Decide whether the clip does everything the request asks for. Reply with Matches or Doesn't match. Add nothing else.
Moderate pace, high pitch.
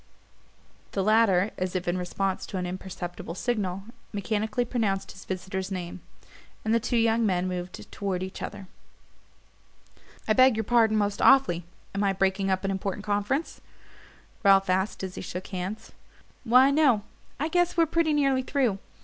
Matches